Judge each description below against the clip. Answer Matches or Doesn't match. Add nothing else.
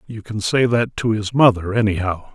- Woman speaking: Doesn't match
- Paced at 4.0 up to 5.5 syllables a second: Matches